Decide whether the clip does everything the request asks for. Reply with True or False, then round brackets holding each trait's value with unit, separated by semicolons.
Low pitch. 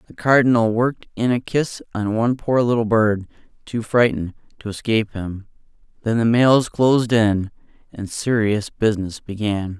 True (110 Hz)